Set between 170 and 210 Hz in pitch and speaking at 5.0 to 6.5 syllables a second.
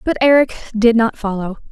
No: high, 230 Hz; 5.4 syllables/s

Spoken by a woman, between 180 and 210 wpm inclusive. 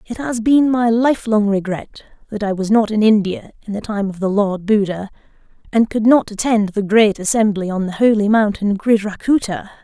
Yes: female; average, 190 wpm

